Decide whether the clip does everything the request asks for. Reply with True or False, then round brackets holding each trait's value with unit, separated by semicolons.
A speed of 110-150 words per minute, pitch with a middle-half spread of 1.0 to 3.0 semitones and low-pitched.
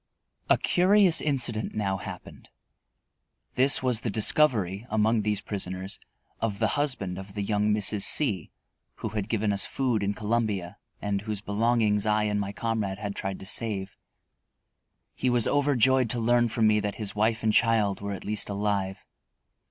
False (165 wpm; 2.5 semitones; 105 Hz)